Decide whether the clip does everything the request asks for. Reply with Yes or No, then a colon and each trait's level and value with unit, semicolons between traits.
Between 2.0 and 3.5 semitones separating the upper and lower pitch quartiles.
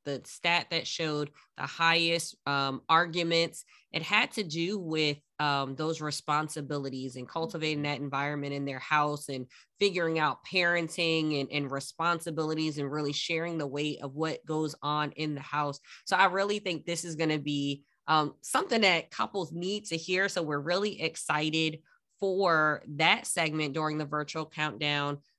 Yes: narrow, 2.4 semitones